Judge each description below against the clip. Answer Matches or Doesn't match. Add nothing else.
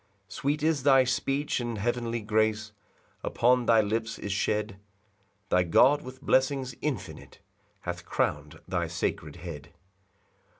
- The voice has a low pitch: Matches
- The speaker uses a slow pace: Matches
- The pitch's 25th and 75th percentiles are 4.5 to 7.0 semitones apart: Doesn't match